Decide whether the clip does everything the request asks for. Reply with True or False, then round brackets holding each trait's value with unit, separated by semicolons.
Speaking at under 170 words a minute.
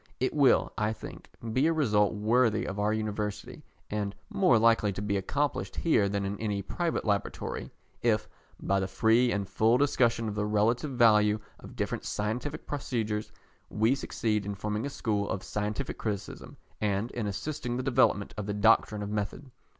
False (175 wpm)